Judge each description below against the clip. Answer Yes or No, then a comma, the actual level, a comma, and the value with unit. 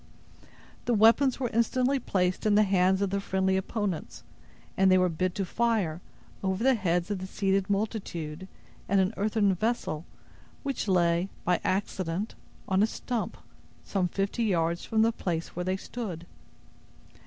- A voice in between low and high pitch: No, high, 195 Hz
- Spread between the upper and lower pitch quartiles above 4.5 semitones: No, average, 3.2 semitones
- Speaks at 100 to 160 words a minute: Yes, average, 155 wpm